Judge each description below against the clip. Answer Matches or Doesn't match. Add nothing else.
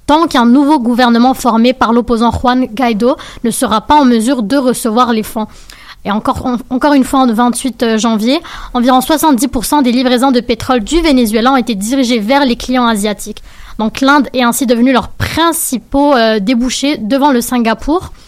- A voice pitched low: Doesn't match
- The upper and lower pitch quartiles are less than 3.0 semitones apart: Matches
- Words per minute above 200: Doesn't match